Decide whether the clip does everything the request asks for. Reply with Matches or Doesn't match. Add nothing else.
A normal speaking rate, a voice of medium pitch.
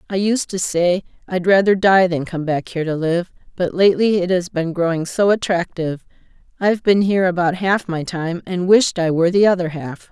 Doesn't match